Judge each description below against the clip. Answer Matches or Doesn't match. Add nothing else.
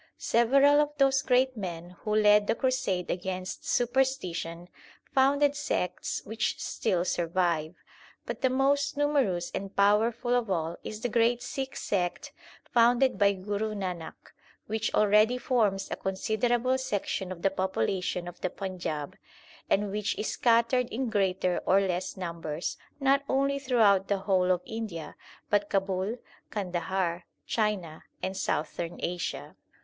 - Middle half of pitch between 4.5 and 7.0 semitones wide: Matches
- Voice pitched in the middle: Doesn't match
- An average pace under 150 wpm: Matches